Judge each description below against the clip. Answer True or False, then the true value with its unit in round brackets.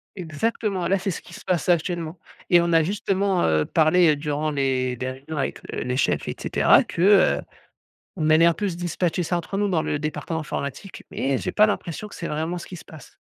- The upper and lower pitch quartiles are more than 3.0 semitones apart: True (3.5 semitones)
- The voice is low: False (170 Hz)